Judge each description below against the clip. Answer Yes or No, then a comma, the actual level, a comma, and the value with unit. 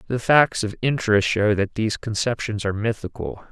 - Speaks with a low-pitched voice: Yes, low, 110 Hz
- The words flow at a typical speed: Yes, average, 170 wpm